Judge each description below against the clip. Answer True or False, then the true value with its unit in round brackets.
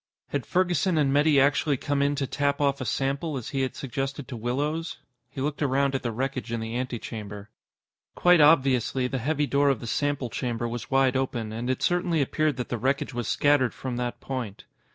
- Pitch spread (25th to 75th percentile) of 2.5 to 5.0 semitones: True (2.9 semitones)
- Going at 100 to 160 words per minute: False (205 wpm)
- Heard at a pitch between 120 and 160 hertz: True (135 Hz)